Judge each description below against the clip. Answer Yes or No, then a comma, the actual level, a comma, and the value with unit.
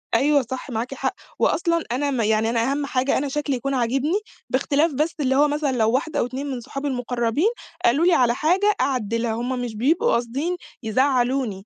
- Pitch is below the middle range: No, very high, 265 Hz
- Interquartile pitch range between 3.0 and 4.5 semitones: Yes, average, 3.5 semitones